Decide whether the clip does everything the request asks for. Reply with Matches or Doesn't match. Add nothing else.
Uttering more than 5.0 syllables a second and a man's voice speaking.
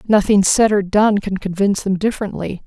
Doesn't match